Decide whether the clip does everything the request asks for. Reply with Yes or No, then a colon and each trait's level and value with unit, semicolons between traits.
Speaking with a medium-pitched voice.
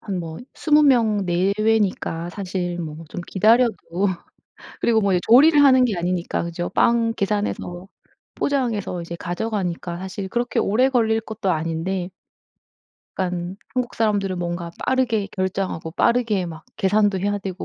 No: high, 195 Hz